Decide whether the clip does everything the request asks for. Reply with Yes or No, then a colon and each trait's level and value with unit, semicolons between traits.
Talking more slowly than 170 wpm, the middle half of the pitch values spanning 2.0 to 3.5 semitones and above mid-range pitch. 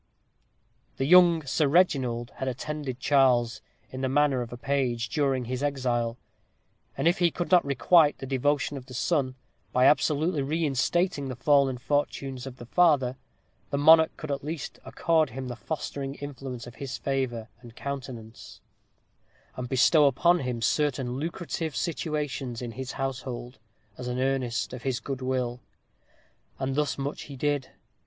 No: average, 155 wpm; average, 2.9 semitones; low, 135 Hz